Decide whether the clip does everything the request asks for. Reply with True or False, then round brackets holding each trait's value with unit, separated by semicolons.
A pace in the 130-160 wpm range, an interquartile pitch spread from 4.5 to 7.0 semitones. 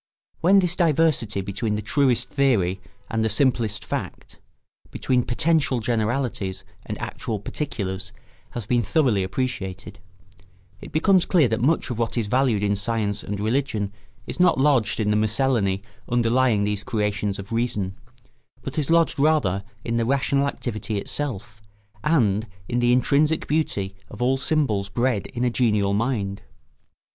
True (150 wpm; 4.9 semitones)